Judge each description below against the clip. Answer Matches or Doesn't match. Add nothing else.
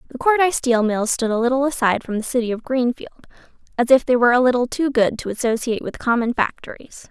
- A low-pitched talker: Doesn't match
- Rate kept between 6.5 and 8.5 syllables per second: Matches